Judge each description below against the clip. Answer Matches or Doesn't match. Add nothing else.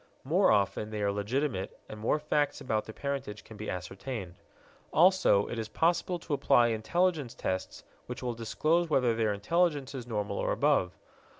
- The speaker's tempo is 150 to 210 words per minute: Matches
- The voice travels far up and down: Matches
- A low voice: Matches